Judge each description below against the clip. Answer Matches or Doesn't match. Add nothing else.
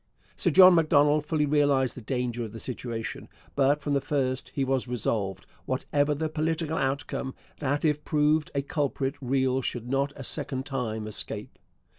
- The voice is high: Doesn't match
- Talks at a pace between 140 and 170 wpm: Matches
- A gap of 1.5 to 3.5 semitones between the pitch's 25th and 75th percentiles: Matches